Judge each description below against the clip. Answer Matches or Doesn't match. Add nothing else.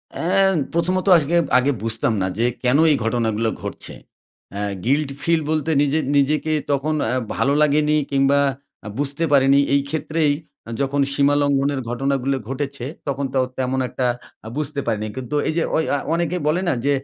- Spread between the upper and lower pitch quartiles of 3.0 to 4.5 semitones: Doesn't match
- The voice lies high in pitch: Doesn't match